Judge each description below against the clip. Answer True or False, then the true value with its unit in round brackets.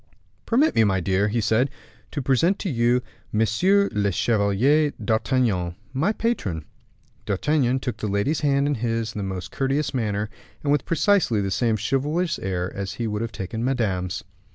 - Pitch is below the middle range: True (115 Hz)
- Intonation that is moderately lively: False (5.8 semitones)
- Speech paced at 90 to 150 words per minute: False (170 wpm)